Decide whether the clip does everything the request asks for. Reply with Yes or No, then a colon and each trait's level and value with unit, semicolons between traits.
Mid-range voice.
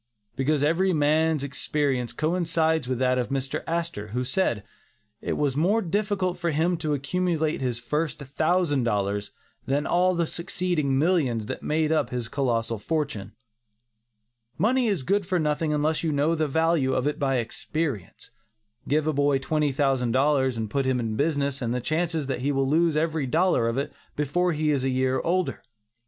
Yes: medium, 150 Hz